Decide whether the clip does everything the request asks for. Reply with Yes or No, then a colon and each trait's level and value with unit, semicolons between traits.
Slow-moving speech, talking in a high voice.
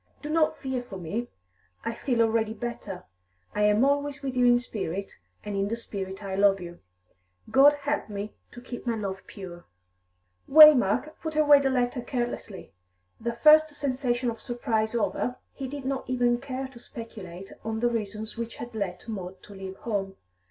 No: average, 175 wpm; high, 235 Hz